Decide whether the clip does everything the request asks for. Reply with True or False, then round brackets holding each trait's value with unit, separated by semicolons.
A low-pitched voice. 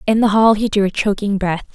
False (205 Hz)